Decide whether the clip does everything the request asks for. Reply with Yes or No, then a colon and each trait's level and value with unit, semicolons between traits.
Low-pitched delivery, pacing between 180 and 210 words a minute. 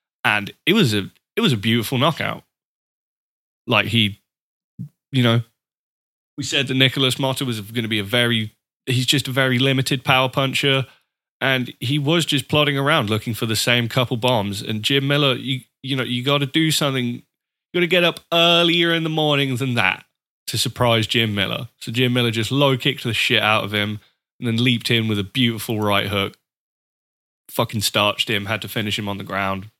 Yes: low, 125 Hz; average, 195 wpm